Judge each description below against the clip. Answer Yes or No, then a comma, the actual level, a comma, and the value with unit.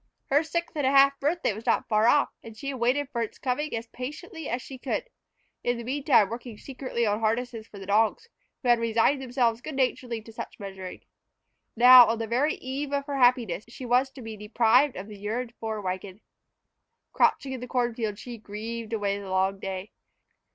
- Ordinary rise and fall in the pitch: Yes, average, 3.5 semitones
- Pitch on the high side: Yes, high, 235 Hz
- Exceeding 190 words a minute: Yes, fast, 205 wpm